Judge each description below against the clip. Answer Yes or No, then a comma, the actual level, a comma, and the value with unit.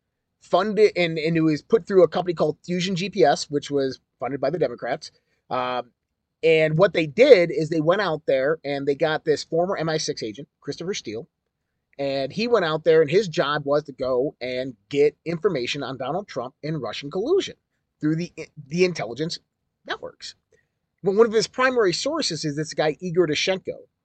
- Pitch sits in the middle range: Yes, medium, 160 Hz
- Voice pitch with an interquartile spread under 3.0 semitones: No, average, 4.7 semitones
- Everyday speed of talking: Yes, average, 180 wpm